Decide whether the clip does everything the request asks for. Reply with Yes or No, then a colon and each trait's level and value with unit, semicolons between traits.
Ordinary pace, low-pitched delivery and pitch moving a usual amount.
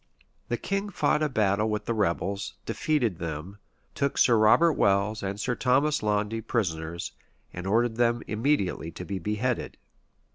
Yes: average, 155 wpm; low, 110 Hz; average, 4.0 semitones